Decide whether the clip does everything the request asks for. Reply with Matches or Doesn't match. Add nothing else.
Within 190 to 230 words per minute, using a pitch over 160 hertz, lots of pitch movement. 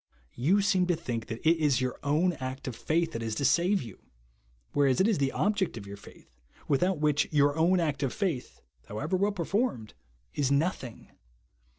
Doesn't match